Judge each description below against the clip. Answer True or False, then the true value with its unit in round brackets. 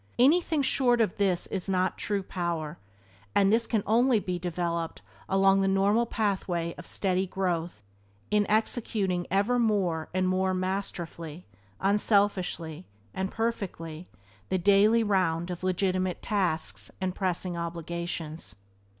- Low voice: False (185 Hz)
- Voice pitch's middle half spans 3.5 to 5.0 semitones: False (3.0 semitones)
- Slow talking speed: True (125 wpm)